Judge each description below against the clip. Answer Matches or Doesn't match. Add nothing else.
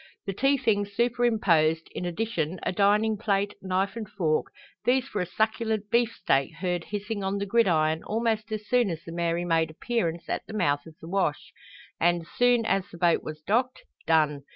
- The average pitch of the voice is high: Matches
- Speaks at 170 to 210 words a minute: Matches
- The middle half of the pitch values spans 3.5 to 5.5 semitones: Matches